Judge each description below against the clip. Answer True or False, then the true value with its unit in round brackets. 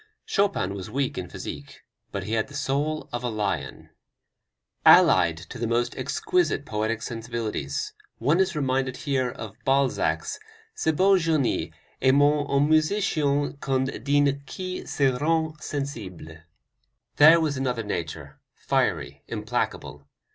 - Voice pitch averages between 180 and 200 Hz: False (135 Hz)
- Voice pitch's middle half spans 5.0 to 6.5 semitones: True (5.3 semitones)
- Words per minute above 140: False (135 wpm)